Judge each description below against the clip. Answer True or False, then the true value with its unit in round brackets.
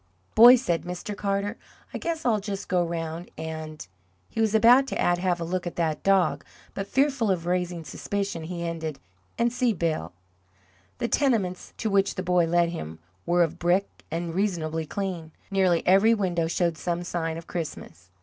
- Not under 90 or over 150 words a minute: False (180 wpm)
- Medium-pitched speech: True (180 Hz)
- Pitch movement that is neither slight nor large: True (3.3 semitones)